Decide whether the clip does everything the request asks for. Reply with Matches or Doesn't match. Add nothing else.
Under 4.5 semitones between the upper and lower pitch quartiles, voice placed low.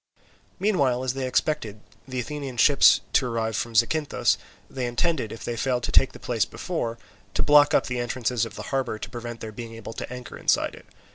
Matches